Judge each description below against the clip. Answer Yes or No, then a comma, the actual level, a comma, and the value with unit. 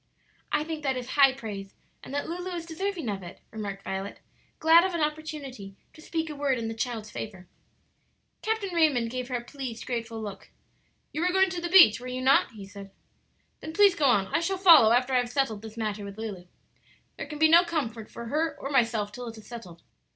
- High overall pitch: Yes, very high, 255 Hz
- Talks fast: Yes, fast, 220 wpm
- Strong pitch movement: Yes, wide, 6.4 semitones